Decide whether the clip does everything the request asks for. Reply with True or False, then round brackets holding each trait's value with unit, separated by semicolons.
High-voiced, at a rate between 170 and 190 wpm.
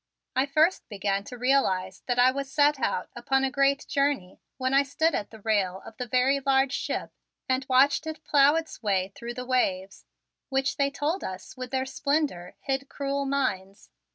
True (265 Hz; 185 wpm)